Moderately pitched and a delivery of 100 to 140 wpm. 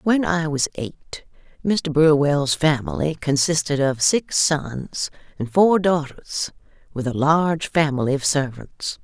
Yes: medium, 150 Hz; slow, 135 wpm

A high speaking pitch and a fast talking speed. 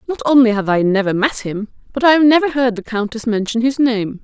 Yes: high, 235 Hz; fast, 240 wpm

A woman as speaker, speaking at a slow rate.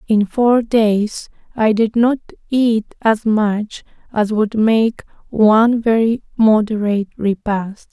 Yes: female; slow, 120 wpm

